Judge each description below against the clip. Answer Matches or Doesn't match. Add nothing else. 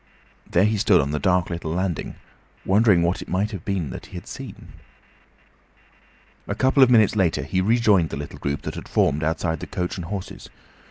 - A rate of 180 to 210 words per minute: Matches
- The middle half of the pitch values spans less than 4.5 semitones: Matches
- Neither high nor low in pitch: Doesn't match